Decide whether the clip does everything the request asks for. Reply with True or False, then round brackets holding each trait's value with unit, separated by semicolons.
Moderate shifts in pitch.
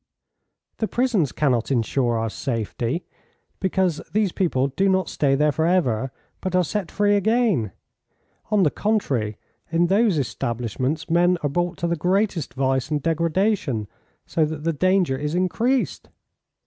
False (6.1 semitones)